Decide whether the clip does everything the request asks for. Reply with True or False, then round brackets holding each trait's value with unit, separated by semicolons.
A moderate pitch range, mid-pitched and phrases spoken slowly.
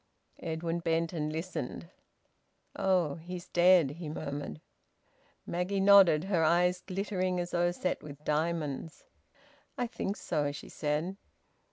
True (3.0 semitones; 170 Hz; 125 wpm)